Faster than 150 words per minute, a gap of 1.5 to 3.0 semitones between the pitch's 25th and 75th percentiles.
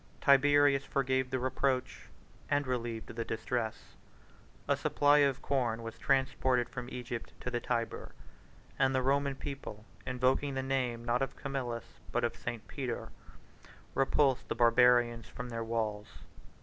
No: average, 140 wpm; narrow, 2.4 semitones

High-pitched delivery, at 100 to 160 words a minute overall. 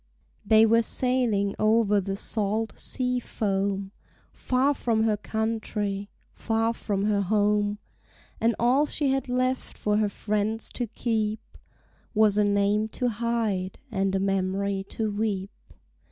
Yes: high, 215 Hz; slow, 135 wpm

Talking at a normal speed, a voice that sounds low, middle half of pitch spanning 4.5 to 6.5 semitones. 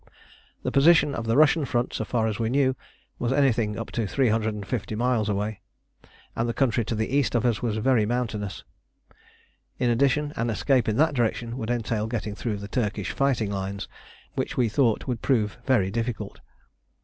No: average, 180 wpm; low, 115 Hz; average, 3.2 semitones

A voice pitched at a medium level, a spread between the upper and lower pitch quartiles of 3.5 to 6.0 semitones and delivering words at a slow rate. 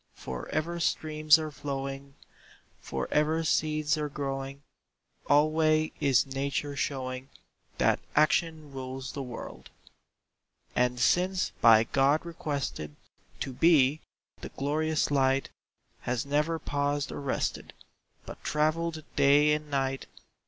No: medium, 145 Hz; narrow, 2.4 semitones; slow, 115 wpm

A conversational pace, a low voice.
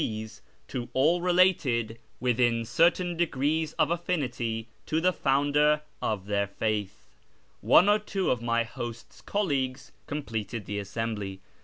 No: slow, 130 wpm; low, 125 Hz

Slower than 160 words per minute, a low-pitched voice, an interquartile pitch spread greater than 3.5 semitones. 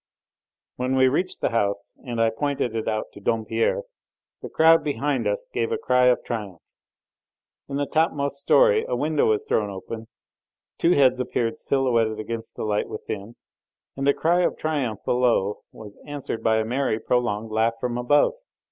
No: average, 170 wpm; low, 125 Hz; average, 4.6 semitones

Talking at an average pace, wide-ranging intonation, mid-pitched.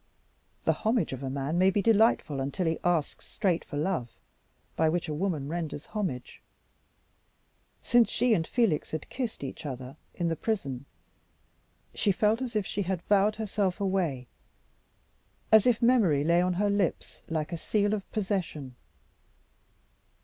Yes: average, 155 wpm; wide, 5.7 semitones; medium, 180 Hz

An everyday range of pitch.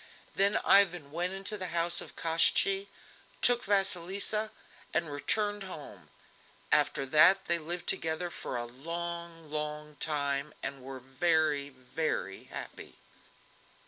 Yes: average, 4.4 semitones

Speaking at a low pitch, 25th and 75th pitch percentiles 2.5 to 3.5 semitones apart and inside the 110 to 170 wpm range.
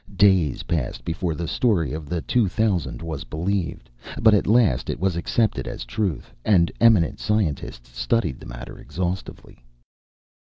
No: very low, 85 Hz; average, 4.9 semitones; average, 150 wpm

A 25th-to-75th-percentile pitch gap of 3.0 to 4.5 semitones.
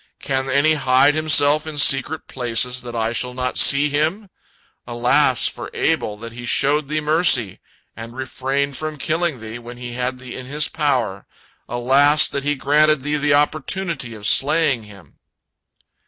Yes: average, 3.5 semitones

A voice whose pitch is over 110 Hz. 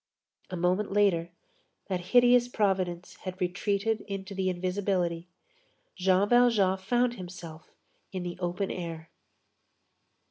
Yes: medium, 185 Hz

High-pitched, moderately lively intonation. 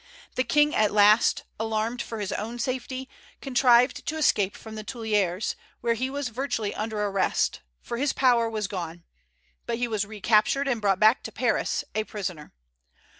Yes: high, 225 Hz; average, 3.3 semitones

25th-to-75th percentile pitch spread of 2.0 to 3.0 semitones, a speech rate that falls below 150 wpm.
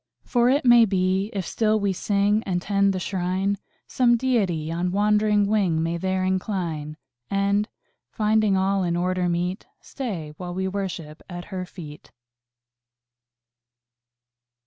Yes: average, 2.7 semitones; slow, 135 wpm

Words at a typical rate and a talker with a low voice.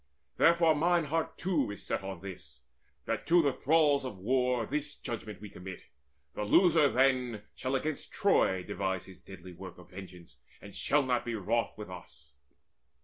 Yes: average, 170 wpm; low, 120 Hz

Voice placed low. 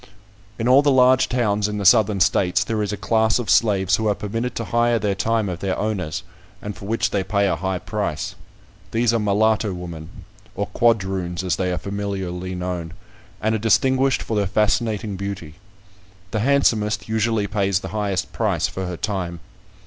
Yes: low, 105 Hz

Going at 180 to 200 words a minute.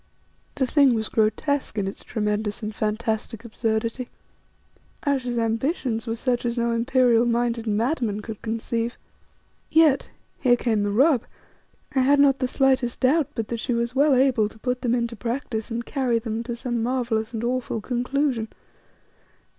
No: average, 160 wpm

